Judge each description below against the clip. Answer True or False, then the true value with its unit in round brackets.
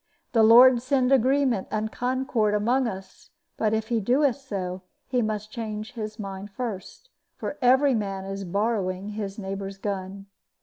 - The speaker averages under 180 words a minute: True (150 wpm)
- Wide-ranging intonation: False (4.1 semitones)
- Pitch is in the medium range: False (215 Hz)